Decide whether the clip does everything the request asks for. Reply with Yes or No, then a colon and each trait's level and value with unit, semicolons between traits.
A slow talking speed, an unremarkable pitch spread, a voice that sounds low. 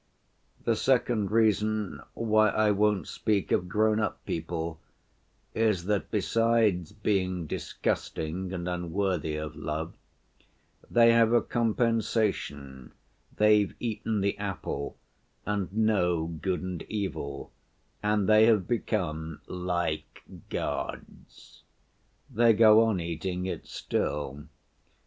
Yes: slow, 105 wpm; average, 3.9 semitones; low, 100 Hz